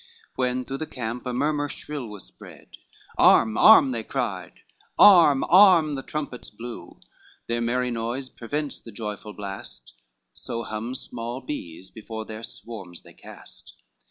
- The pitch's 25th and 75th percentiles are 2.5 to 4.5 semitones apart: Yes, average, 3.7 semitones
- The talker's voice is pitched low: Yes, low, 120 Hz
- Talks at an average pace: Yes, average, 145 wpm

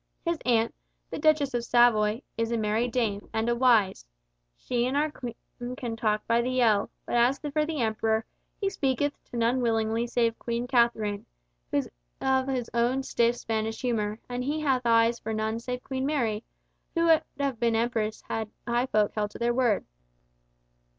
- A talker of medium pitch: No, high, 235 Hz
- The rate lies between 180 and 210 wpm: Yes, average, 185 wpm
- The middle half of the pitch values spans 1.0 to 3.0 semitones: Yes, narrow, 2.5 semitones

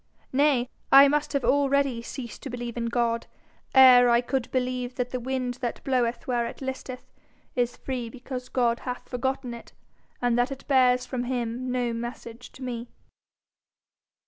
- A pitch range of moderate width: No, narrow, 1.5 semitones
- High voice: Yes, very high, 250 Hz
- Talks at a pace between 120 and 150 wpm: No, average, 165 wpm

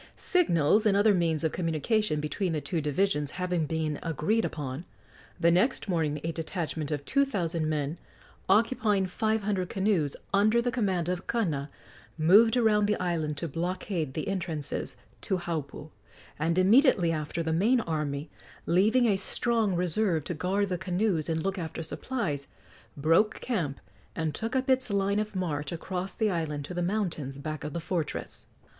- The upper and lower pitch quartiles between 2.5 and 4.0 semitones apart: No, average, 4.8 semitones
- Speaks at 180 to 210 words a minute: No, average, 165 wpm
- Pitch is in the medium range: Yes, medium, 175 Hz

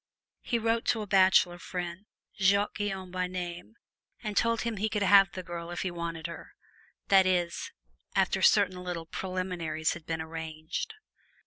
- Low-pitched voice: No, medium, 185 Hz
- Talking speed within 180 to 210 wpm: No, average, 160 wpm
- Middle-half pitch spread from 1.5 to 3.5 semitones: Yes, average, 2.8 semitones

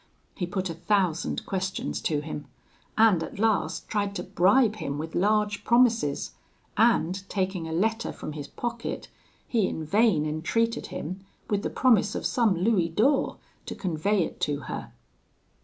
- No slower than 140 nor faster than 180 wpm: Yes, average, 155 wpm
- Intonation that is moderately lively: Yes, average, 5.0 semitones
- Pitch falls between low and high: No, high, 195 Hz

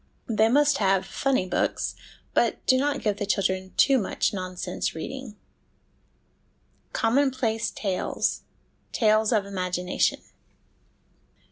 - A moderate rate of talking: No, slow, 110 wpm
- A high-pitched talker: Yes, high, 215 Hz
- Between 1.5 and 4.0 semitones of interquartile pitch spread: No, wide, 5.5 semitones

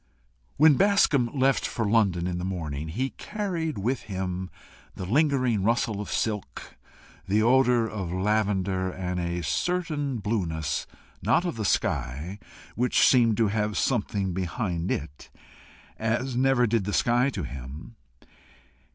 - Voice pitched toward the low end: Yes, low, 105 Hz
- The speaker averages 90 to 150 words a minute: Yes, slow, 135 wpm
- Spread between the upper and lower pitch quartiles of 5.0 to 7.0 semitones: Yes, wide, 5.5 semitones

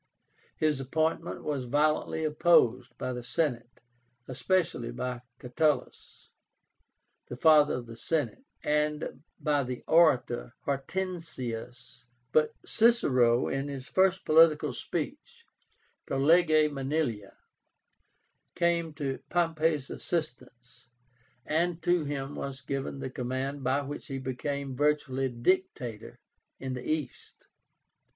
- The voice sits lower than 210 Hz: Yes, medium, 140 Hz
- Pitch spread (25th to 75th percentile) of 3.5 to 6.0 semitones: Yes, average, 3.8 semitones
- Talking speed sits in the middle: No, slow, 110 wpm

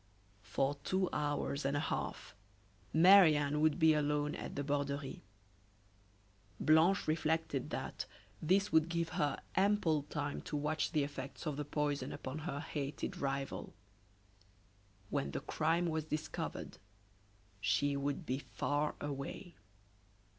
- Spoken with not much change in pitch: Yes, narrow, 2.1 semitones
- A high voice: No, medium, 150 Hz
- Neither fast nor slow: No, slow, 130 wpm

